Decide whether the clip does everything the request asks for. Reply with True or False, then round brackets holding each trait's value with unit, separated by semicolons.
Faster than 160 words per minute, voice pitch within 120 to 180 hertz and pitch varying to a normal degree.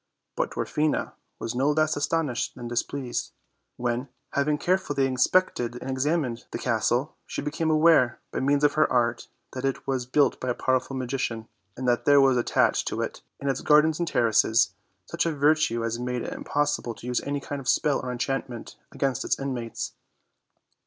True (180 wpm; 135 Hz; 3.2 semitones)